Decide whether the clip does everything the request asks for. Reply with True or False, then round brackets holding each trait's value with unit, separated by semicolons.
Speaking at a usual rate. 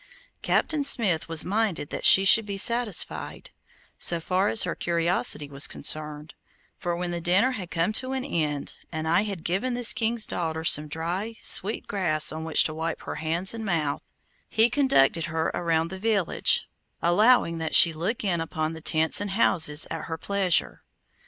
True (180 wpm)